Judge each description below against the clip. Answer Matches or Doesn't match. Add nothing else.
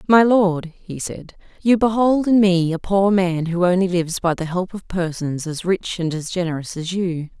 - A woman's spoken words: Matches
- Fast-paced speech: Matches